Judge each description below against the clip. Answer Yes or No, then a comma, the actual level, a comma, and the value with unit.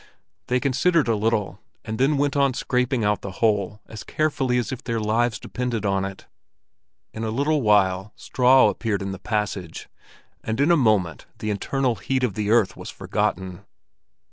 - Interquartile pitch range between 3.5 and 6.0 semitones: Yes, average, 4.0 semitones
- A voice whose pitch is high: No, low, 110 Hz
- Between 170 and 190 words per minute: Yes, average, 175 wpm